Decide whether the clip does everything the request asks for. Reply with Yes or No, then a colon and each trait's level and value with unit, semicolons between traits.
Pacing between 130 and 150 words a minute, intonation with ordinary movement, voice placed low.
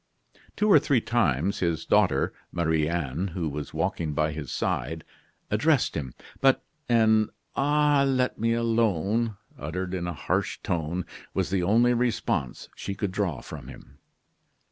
No: average, 145 wpm; wide, 6.5 semitones; very low, 95 Hz